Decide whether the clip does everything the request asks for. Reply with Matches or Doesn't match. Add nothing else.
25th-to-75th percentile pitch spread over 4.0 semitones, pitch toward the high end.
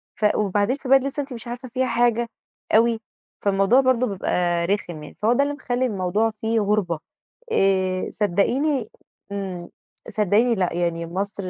Matches